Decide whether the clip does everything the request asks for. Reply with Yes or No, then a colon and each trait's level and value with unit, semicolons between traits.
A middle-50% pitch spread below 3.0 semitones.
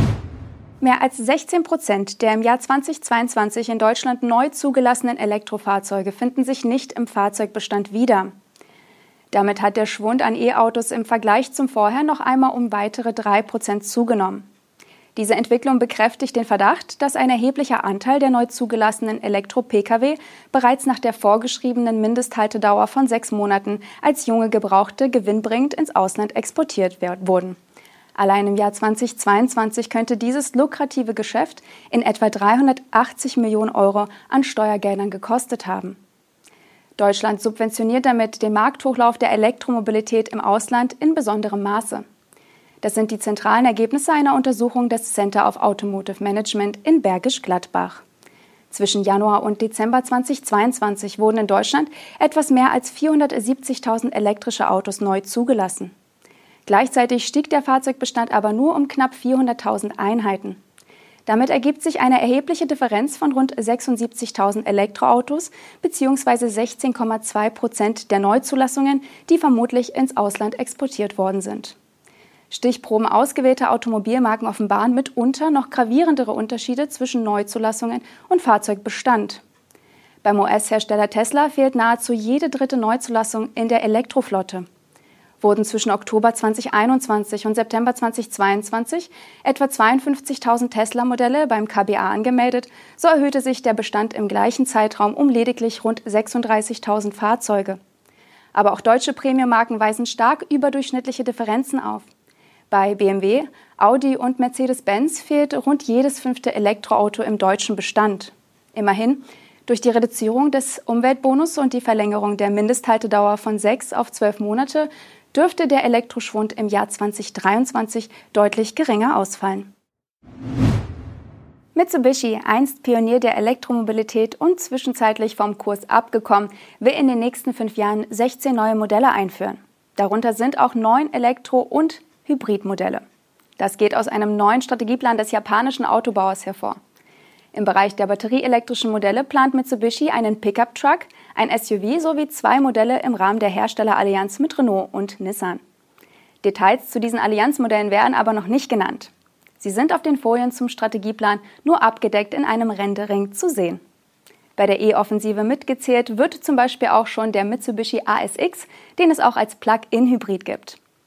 No: average, 3.6 semitones